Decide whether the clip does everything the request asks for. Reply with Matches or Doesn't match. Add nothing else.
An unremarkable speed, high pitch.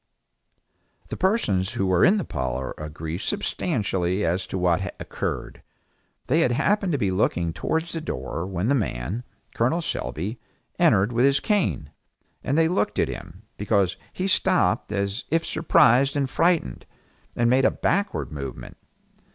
Doesn't match